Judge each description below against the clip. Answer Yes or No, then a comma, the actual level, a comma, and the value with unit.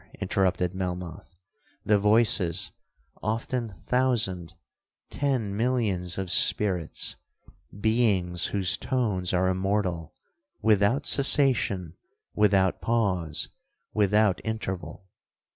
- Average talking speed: No, slow, 75 wpm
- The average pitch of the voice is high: No, low, 100 Hz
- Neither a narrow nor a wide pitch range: Yes, average, 3.6 semitones